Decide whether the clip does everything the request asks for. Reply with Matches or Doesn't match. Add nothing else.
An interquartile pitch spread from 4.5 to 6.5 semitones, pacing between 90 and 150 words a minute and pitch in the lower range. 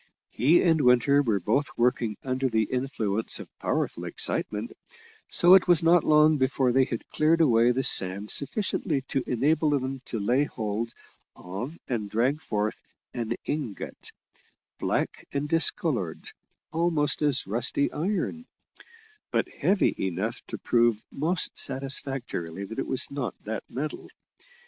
Matches